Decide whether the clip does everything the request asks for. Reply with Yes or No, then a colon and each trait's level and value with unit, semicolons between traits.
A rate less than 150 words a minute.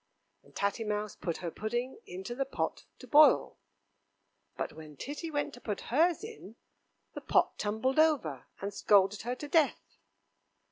No: average, 155 wpm